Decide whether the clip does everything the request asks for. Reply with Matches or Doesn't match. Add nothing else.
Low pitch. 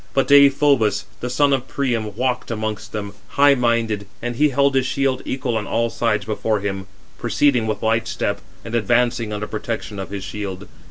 Matches